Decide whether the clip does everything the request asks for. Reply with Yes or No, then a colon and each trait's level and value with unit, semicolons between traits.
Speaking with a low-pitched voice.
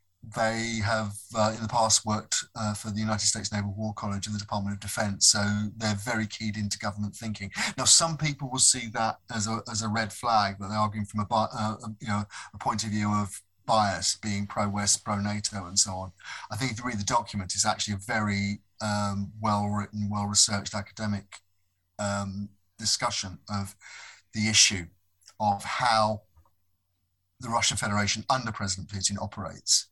Yes: low, 105 Hz